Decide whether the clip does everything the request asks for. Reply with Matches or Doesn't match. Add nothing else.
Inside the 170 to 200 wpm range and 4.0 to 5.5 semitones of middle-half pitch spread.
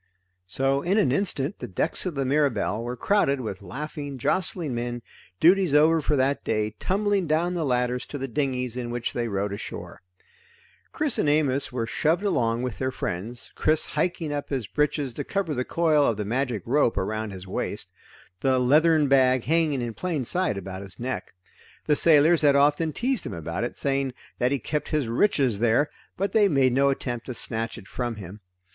Matches